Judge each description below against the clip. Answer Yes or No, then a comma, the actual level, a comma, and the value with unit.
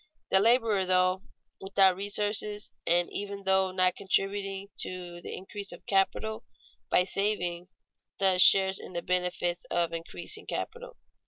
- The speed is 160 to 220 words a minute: No, slow, 135 wpm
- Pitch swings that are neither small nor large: No, narrow, 1.8 semitones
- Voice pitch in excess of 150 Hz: Yes, high, 190 Hz